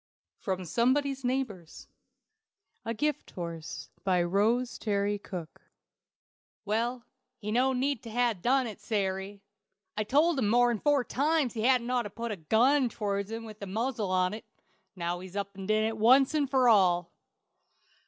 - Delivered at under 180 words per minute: Yes, average, 155 wpm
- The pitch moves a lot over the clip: No, average, 4.2 semitones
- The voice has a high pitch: Yes, high, 220 Hz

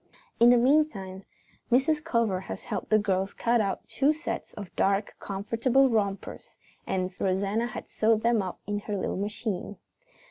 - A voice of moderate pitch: No, high, 210 Hz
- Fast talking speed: No, average, 155 wpm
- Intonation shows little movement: No, average, 3.5 semitones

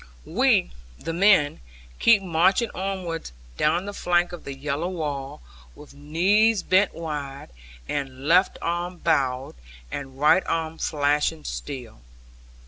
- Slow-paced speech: Yes, slow, 125 wpm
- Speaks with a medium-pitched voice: Yes, medium, 160 Hz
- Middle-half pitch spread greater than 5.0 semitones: No, average, 4.2 semitones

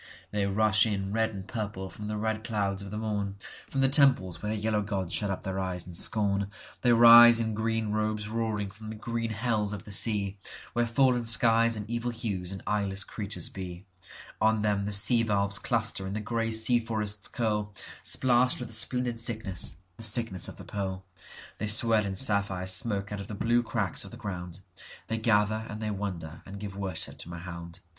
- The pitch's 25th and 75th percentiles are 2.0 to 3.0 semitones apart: Yes, narrow, 2.5 semitones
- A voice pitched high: No, low, 105 Hz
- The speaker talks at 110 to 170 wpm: No, average, 185 wpm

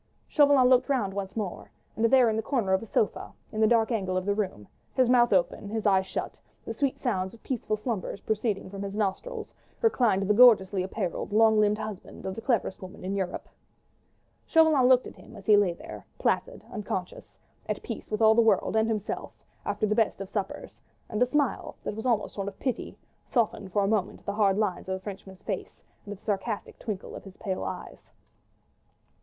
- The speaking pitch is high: Yes, high, 210 Hz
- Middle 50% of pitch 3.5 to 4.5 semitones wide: No, average, 3.1 semitones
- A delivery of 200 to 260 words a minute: Yes, fast, 205 wpm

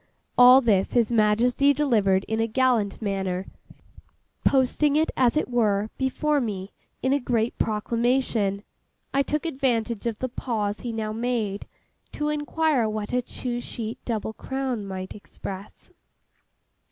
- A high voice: Yes, high, 235 Hz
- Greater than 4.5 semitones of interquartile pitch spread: No, average, 3.8 semitones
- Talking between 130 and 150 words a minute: Yes, average, 140 wpm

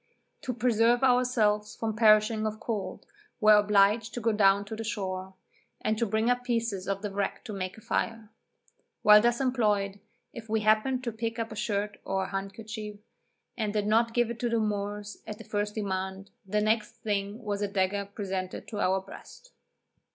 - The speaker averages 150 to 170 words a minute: No, average, 185 wpm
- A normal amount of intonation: No, narrow, 2.2 semitones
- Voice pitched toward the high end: Yes, high, 215 Hz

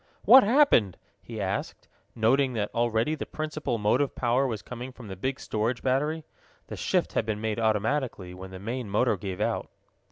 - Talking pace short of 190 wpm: Yes, average, 180 wpm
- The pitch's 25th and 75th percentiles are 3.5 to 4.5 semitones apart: Yes, average, 4.2 semitones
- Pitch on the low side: Yes, low, 120 Hz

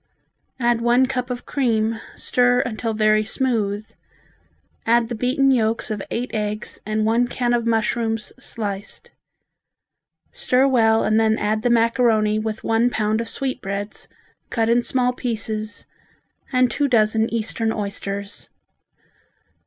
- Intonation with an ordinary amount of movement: No, narrow, 2.3 semitones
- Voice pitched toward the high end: Yes, high, 225 Hz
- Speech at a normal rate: No, slow, 130 wpm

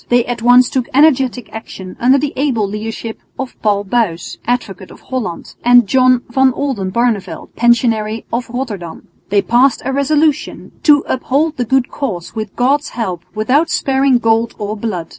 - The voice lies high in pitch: Yes, high, 240 Hz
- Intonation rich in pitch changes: No, average, 3.6 semitones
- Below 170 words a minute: Yes, average, 160 wpm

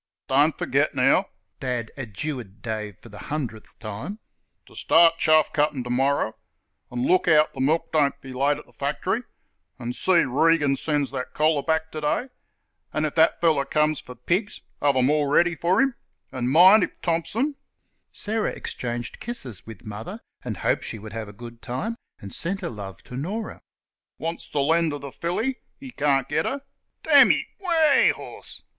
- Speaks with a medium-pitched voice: Yes, medium, 145 Hz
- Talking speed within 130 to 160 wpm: No, average, 175 wpm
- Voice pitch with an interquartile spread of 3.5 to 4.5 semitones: No, wide, 5.4 semitones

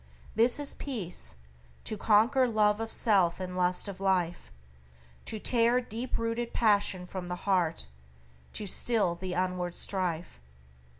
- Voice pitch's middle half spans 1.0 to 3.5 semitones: No, average, 4.1 semitones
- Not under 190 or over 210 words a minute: No, slow, 135 wpm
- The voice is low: No, high, 200 Hz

